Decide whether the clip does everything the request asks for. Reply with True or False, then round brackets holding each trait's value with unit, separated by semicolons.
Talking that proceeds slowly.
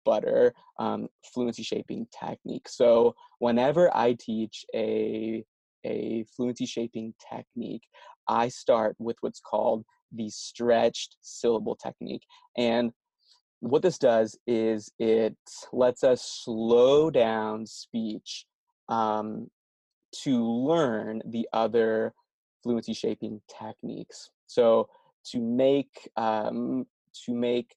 True (105 wpm)